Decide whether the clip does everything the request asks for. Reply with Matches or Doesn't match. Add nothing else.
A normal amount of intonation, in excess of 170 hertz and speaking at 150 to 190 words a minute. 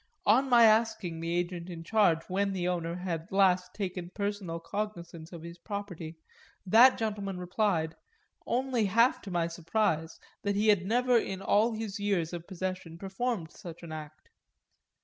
Matches